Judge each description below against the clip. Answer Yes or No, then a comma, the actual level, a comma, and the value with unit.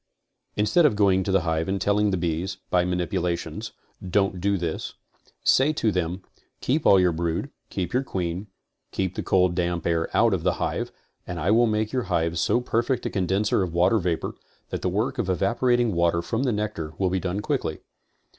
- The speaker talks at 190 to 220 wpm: Yes, average, 200 wpm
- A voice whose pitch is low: Yes, very low, 95 Hz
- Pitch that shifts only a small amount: No, average, 3.6 semitones